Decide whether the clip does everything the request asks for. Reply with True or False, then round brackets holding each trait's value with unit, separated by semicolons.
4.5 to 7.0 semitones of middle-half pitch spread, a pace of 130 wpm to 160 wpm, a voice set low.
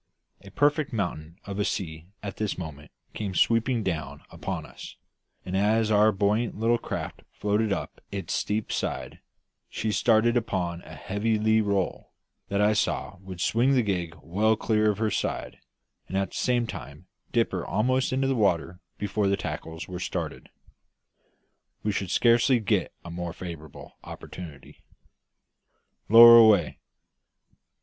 False (3.8 semitones; 150 wpm; 105 Hz)